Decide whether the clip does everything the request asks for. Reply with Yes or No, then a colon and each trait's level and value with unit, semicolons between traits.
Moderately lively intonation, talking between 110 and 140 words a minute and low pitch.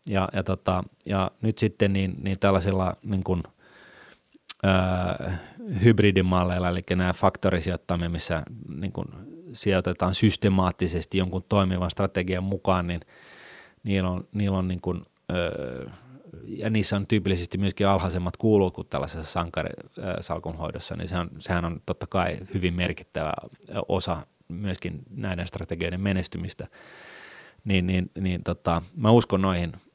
No: narrow, 1.6 semitones; average, 120 wpm; very low, 95 Hz